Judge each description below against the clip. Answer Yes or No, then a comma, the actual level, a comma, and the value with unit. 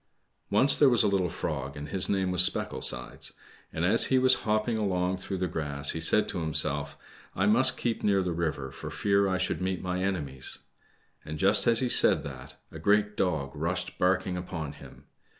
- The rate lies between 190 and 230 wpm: Yes, average, 200 wpm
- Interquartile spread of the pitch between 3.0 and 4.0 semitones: No, average, 4.6 semitones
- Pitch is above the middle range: No, very low, 90 Hz